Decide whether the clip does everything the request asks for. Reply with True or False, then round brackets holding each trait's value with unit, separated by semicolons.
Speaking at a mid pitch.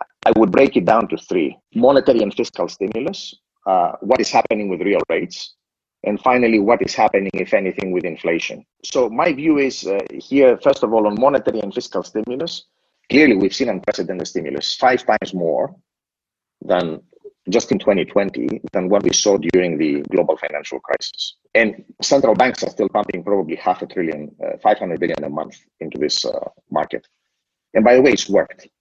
False (110 Hz)